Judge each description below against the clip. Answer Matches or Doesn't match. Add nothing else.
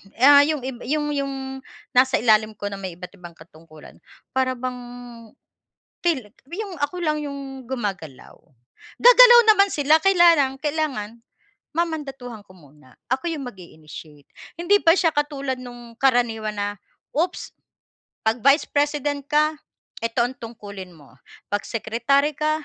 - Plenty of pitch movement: Matches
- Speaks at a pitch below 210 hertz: Doesn't match